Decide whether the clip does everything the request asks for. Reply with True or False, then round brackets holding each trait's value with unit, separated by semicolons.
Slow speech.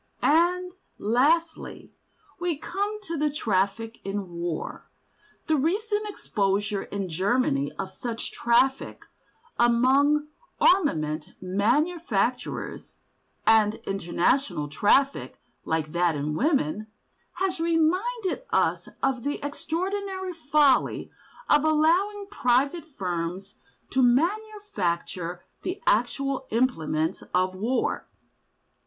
True (90 wpm)